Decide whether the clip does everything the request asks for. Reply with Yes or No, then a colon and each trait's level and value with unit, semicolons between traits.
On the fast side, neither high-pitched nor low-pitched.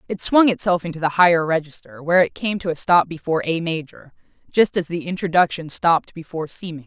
Yes: fast, 210 wpm; medium, 170 Hz